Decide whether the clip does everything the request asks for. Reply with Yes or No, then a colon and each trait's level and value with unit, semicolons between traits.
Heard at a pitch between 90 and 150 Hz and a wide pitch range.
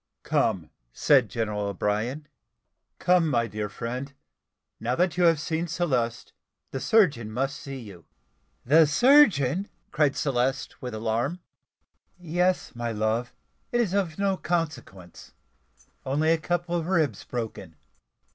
Yes: medium, 140 Hz; wide, 6.7 semitones